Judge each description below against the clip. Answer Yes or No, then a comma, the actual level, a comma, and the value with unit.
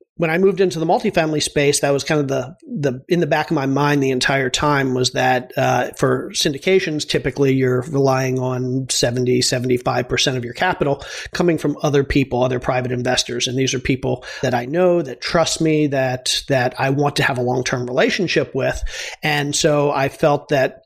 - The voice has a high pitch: No, medium, 140 Hz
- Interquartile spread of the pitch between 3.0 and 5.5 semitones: Yes, average, 3.4 semitones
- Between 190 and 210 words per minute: Yes, average, 200 wpm